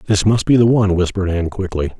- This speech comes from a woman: No, male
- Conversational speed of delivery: No, fast, 240 wpm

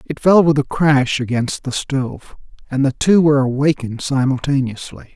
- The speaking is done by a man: Yes, male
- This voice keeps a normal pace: Yes, average, 165 wpm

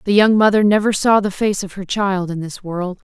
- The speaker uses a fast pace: Yes, fast, 250 wpm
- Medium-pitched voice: No, high, 195 Hz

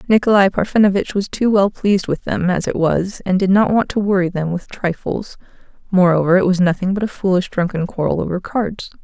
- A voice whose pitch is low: No, high, 190 Hz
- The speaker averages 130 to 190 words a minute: No, fast, 205 wpm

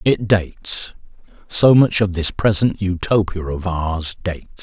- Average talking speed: No, slow, 130 wpm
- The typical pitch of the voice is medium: No, very low, 95 Hz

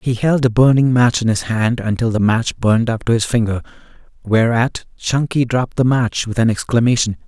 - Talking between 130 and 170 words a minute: No, average, 200 wpm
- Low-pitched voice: Yes, low, 115 Hz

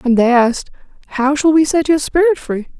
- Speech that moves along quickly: Yes, fast, 215 wpm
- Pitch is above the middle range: Yes, very high, 280 Hz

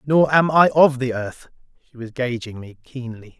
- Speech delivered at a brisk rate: No, average, 195 wpm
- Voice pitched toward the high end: No, low, 130 Hz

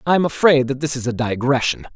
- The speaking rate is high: Yes, fast, 245 wpm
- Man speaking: Yes, male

